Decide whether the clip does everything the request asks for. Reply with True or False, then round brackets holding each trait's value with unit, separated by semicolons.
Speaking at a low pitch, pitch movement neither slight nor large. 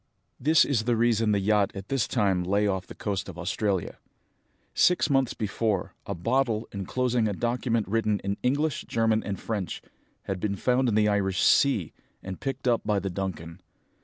True (105 Hz; 3.6 semitones)